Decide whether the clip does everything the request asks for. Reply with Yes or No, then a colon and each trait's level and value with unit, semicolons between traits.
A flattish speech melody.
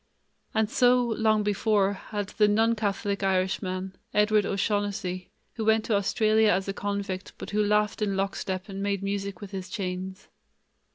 Yes: narrow, 1.7 semitones